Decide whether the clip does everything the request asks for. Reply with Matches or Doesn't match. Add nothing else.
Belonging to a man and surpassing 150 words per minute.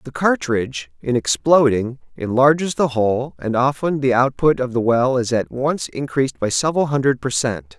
Matches